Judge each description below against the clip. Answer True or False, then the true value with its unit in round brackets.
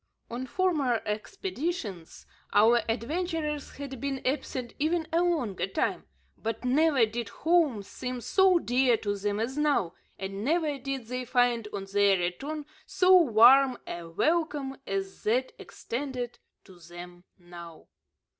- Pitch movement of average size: False (6.6 semitones)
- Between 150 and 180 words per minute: False (135 wpm)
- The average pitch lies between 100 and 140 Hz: False (250 Hz)